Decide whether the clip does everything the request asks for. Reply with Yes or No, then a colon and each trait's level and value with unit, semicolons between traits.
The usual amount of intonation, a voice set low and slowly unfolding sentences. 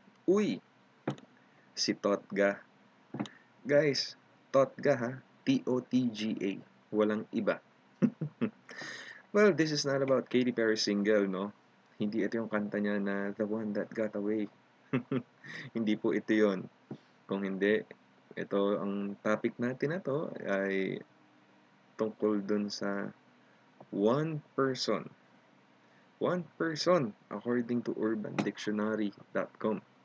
Yes: average, 4.1 semitones; low, 110 Hz; slow, 105 wpm